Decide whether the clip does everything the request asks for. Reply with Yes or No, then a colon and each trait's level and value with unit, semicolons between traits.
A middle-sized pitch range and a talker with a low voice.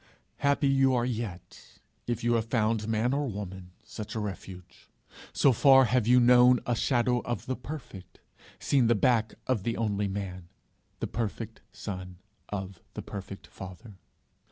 Yes: average, 4.0 semitones; low, 115 Hz